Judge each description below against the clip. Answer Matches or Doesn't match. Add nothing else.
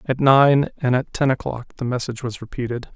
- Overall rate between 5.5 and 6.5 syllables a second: Matches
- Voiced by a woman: Doesn't match